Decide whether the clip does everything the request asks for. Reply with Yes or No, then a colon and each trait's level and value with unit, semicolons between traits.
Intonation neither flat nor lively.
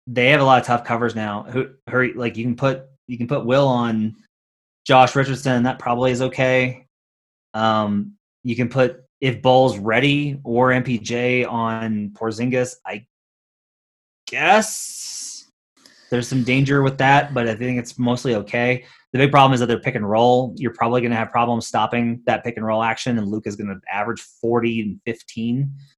No: narrow, 2.2 semitones